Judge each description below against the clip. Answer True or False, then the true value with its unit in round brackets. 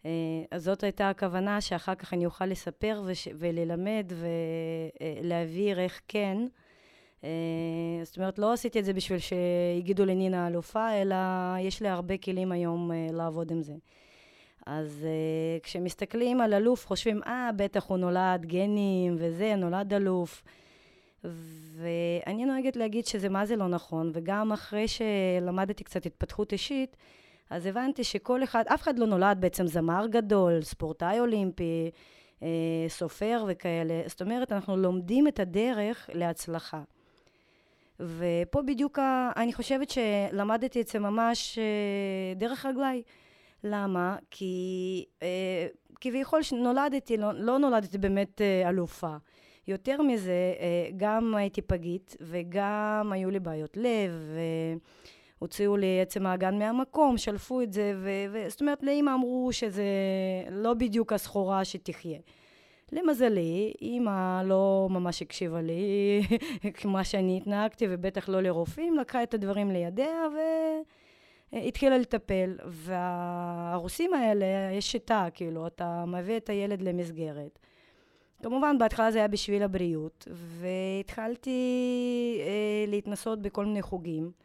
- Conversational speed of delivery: True (125 wpm)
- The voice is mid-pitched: False (195 Hz)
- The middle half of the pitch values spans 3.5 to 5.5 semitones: True (4.3 semitones)